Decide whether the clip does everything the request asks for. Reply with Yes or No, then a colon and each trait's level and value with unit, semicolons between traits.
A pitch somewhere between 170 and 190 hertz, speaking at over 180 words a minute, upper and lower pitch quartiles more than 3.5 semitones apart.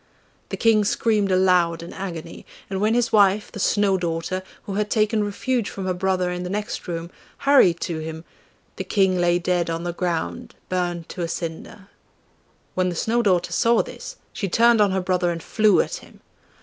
No: medium, 185 Hz; average, 190 wpm; average, 3.2 semitones